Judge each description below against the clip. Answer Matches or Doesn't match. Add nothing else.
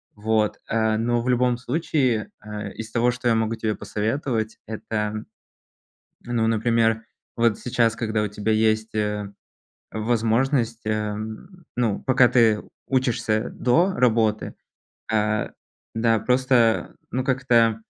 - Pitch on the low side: Matches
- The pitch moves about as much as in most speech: Doesn't match